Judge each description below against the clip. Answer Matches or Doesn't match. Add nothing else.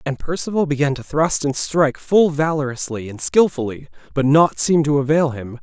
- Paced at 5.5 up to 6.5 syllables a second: Doesn't match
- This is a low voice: Doesn't match